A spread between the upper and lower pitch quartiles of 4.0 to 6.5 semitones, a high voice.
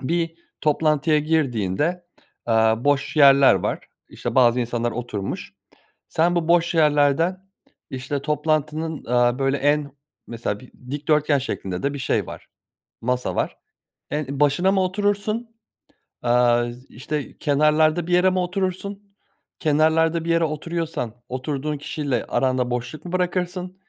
No: average, 4.6 semitones; medium, 150 Hz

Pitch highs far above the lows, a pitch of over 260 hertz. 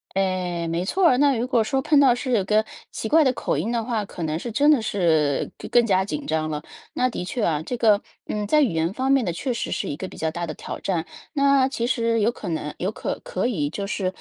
No: wide, 6.6 semitones; high, 215 Hz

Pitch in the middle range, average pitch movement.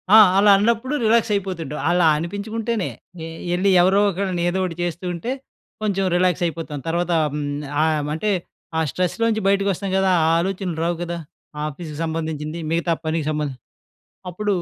Yes: medium, 180 Hz; average, 3.5 semitones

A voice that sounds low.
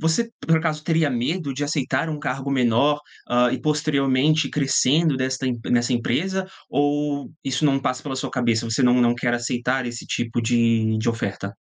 Yes: low, 130 Hz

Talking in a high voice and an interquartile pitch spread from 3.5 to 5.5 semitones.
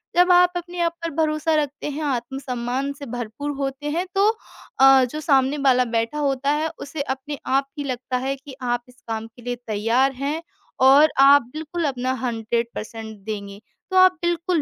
Yes: very high, 275 Hz; average, 3.8 semitones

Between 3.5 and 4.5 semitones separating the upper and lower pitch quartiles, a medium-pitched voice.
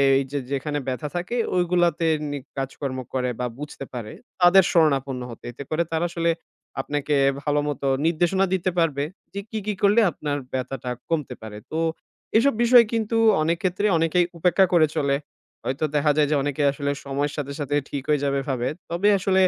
Yes: average, 4.1 semitones; medium, 150 Hz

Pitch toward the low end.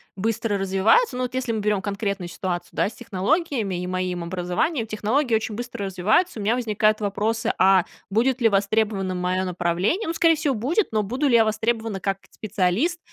No: high, 215 Hz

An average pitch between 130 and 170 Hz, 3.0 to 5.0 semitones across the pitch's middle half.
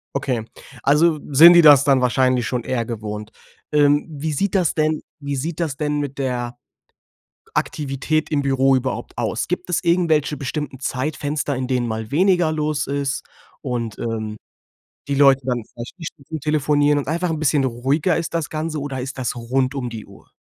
Yes: medium, 140 Hz; average, 3.3 semitones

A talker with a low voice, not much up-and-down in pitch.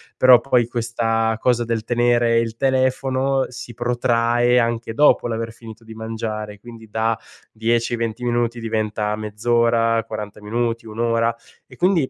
Yes: low, 115 Hz; narrow, 1.2 semitones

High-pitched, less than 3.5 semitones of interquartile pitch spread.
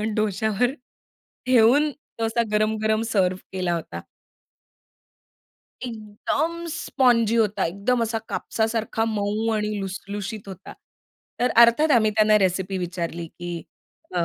Yes: high, 215 Hz; average, 3.1 semitones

